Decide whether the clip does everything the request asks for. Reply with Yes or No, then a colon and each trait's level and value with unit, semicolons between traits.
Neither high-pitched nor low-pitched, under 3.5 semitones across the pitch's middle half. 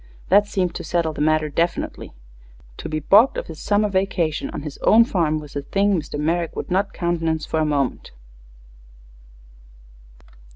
No: medium, 165 Hz; average, 3.9 semitones